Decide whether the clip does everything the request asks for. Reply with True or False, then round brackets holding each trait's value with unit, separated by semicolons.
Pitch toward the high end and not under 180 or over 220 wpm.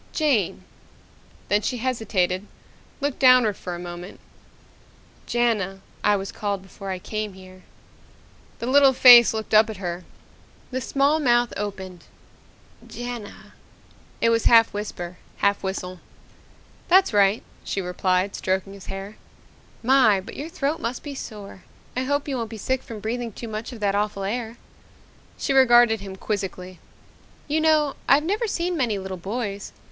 False (215 Hz; 150 wpm)